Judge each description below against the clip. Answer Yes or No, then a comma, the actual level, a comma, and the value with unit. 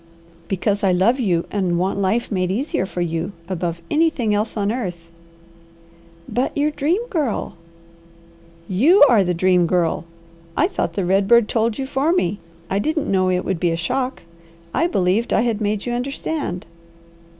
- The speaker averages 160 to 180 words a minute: Yes, average, 170 wpm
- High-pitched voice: Yes, high, 205 Hz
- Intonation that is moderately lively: No, wide, 5.7 semitones